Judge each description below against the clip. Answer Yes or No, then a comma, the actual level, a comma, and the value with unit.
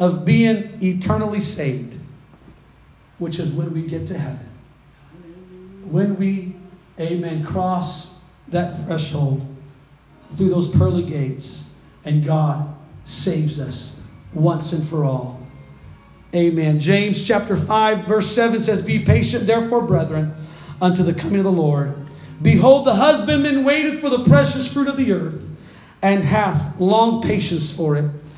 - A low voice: No, medium, 170 Hz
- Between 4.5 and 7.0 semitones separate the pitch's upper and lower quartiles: Yes, average, 4.8 semitones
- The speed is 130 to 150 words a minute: Yes, slow, 135 wpm